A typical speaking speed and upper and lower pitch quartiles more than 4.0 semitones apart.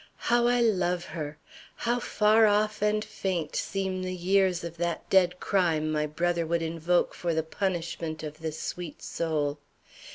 No: average, 160 wpm; average, 3.5 semitones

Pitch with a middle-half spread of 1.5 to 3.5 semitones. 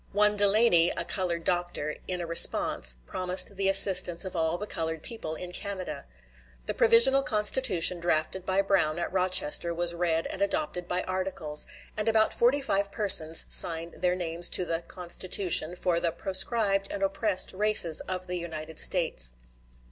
Yes: average, 2.8 semitones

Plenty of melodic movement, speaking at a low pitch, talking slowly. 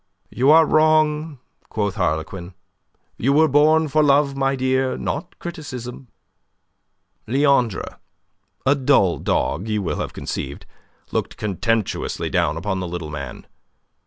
Yes: wide, 7.4 semitones; low, 130 Hz; slow, 130 wpm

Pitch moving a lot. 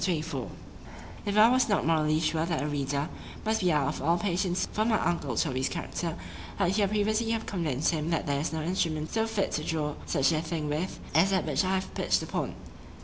No: average, 4.2 semitones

